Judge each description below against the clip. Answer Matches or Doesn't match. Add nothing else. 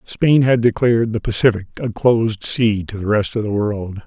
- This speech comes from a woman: Doesn't match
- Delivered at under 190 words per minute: Doesn't match